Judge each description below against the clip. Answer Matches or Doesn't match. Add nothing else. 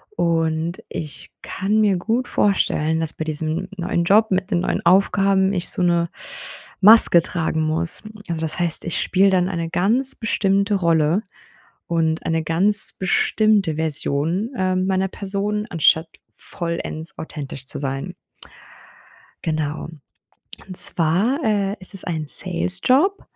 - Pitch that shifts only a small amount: Doesn't match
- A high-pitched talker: Doesn't match